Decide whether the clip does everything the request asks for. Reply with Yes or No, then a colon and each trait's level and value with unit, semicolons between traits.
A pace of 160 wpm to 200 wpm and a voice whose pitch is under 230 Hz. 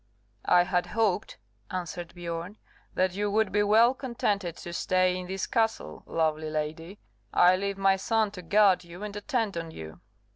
Yes: average, 170 wpm; medium, 185 Hz